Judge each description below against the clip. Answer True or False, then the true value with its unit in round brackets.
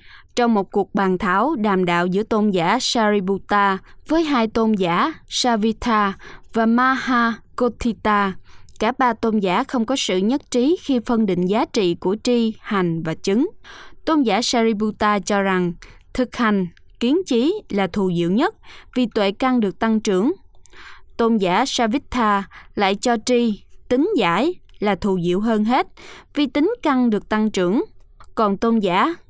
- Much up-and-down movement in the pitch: False (4.1 semitones)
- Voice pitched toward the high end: True (225 Hz)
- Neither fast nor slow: False (160 wpm)